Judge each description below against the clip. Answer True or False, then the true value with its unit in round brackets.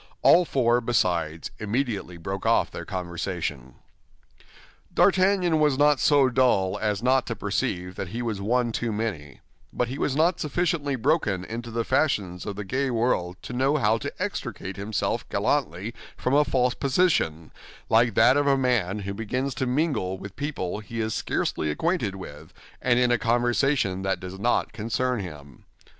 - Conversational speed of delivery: True (165 wpm)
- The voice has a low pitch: True (115 Hz)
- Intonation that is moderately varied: False (5.8 semitones)